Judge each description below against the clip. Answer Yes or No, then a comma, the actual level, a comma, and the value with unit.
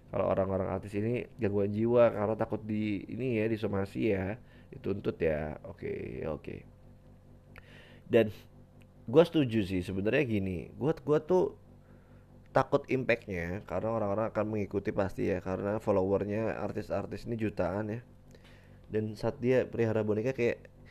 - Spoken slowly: No, fast, 140 wpm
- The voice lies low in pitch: Yes, low, 110 Hz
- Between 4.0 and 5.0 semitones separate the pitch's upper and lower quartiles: No, average, 2.8 semitones